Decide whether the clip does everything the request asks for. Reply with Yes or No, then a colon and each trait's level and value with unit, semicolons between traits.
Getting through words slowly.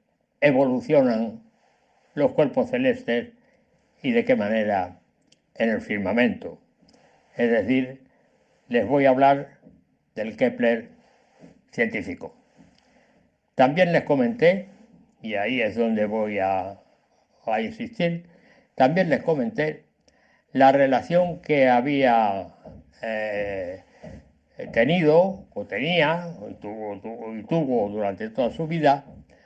Yes: slow, 100 wpm